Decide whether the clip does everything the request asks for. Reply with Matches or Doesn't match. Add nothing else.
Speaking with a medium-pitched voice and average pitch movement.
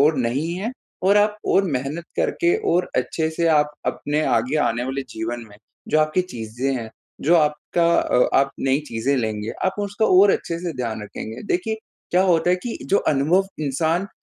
Doesn't match